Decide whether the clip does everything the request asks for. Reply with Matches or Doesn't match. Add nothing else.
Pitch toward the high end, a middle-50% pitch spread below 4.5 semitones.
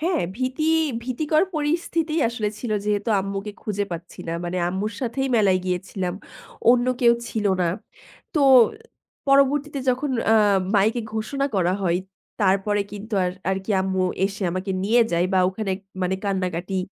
Doesn't match